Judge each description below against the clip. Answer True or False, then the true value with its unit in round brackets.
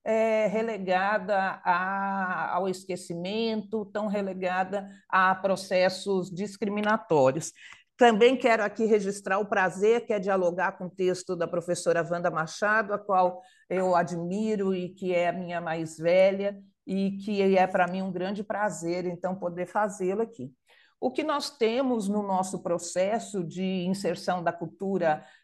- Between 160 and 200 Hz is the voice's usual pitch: True (190 Hz)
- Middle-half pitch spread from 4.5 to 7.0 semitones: False (2.8 semitones)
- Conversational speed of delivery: True (140 wpm)